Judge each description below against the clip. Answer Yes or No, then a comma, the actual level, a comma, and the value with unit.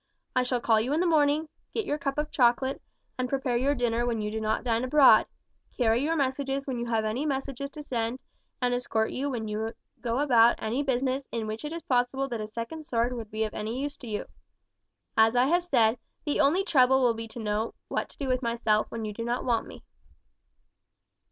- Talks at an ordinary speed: No, fast, 220 wpm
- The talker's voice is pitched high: Yes, high, 245 Hz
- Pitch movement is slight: No, average, 3.4 semitones